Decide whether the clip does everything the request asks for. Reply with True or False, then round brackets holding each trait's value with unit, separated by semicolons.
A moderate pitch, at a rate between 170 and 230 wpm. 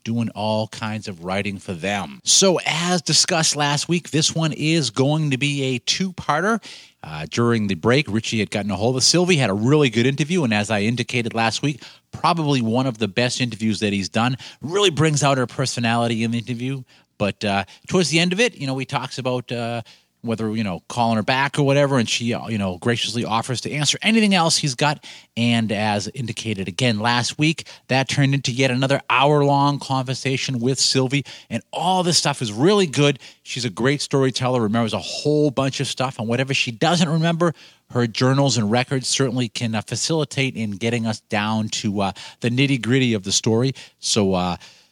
False (125 Hz; 205 wpm)